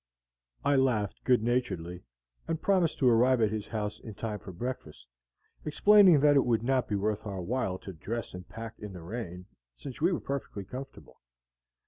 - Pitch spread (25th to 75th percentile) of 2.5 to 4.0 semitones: No, average, 4.8 semitones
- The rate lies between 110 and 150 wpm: No, average, 180 wpm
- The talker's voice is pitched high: No, low, 115 Hz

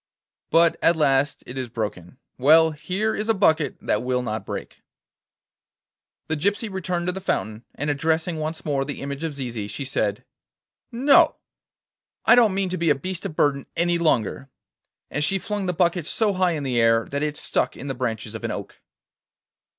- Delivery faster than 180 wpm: Yes, average, 190 wpm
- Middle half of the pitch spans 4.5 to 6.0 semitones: Yes, wide, 5.6 semitones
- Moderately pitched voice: Yes, medium, 150 Hz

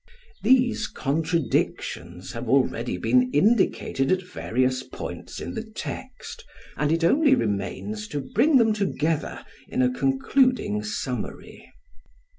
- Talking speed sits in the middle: No, slow, 115 wpm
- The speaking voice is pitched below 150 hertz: Yes, low, 135 Hz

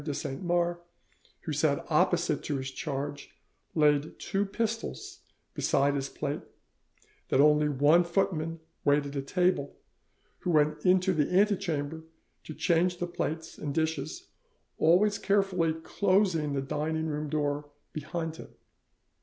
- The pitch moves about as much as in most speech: Yes, average, 3.5 semitones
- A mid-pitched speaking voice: Yes, medium, 160 Hz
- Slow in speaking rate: Yes, slow, 130 wpm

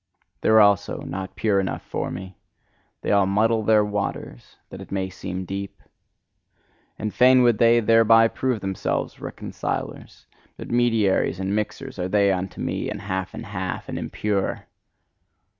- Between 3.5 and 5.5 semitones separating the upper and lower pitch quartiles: No, average, 2.7 semitones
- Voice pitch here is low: Yes, low, 100 Hz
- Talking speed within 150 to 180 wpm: Yes, average, 155 wpm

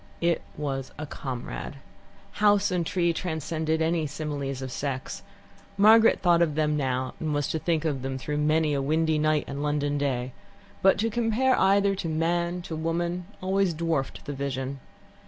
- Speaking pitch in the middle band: Yes, medium, 155 Hz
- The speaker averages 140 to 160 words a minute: No, average, 170 wpm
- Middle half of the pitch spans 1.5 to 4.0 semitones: Yes, average, 3.4 semitones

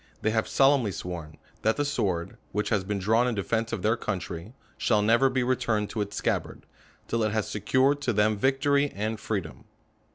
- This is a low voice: Yes, low, 110 Hz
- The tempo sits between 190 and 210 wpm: Yes, average, 195 wpm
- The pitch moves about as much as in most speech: Yes, average, 3.6 semitones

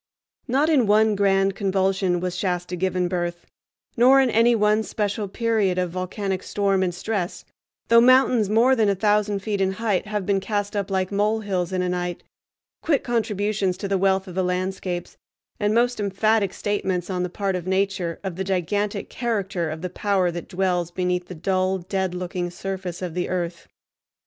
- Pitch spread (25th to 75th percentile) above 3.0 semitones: No, narrow, 2.5 semitones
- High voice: Yes, high, 195 Hz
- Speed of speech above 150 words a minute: Yes, average, 180 wpm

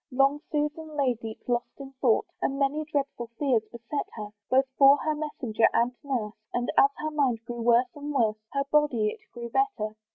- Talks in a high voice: Yes, very high, 265 Hz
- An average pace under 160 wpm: No, average, 190 wpm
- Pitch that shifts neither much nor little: Yes, average, 3.7 semitones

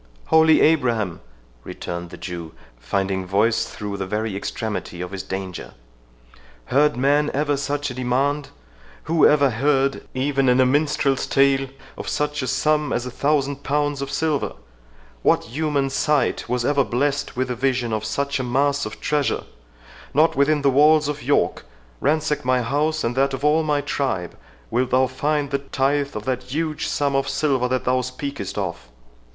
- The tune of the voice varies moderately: Yes, average, 4.3 semitones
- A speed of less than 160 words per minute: No, average, 165 wpm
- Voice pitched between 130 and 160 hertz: Yes, low, 135 Hz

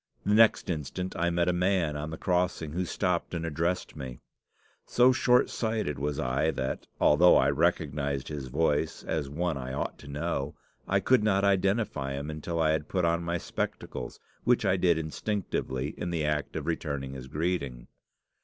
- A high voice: No, very low, 80 Hz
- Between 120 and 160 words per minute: No, average, 180 wpm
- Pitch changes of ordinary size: Yes, average, 3.8 semitones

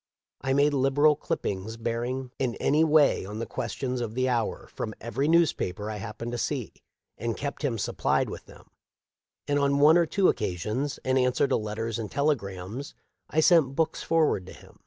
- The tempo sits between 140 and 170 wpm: No, average, 185 wpm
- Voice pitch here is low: Yes, low, 130 Hz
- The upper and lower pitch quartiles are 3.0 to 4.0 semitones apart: No, average, 4.4 semitones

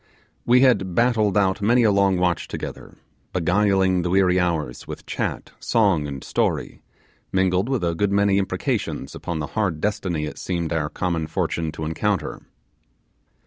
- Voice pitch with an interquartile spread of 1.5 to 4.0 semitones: Yes, average, 3.4 semitones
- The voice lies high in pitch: No, very low, 95 Hz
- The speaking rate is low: No, average, 155 wpm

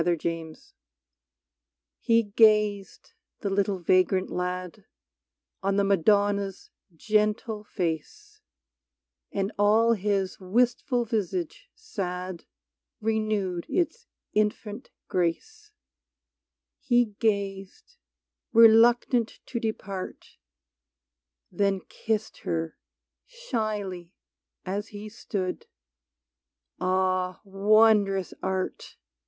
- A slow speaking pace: Yes, slow, 80 wpm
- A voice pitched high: Yes, high, 200 Hz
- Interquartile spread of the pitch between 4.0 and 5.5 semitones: No, average, 2.9 semitones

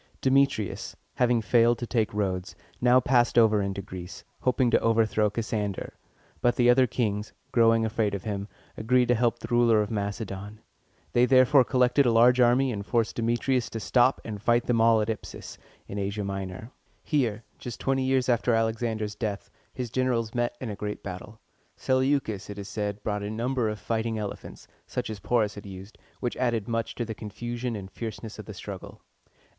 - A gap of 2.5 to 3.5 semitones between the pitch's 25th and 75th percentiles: Yes, average, 2.8 semitones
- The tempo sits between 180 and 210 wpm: Yes, average, 185 wpm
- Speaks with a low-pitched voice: Yes, low, 115 Hz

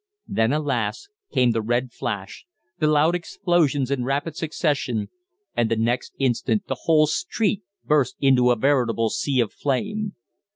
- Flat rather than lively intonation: No, average, 4.6 semitones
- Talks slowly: No, average, 150 wpm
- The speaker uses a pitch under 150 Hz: Yes, medium, 140 Hz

